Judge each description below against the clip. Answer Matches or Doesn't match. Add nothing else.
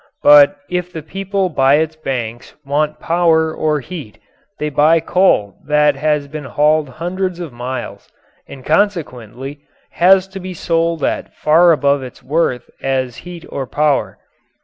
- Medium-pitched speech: Matches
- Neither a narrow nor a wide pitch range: Matches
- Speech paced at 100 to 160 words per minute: Matches